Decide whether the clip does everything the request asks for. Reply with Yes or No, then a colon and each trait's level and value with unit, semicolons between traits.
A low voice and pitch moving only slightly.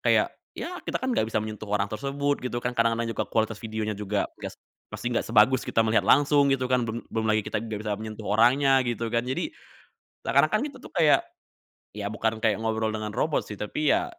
No: low, 115 Hz; average, 3.6 semitones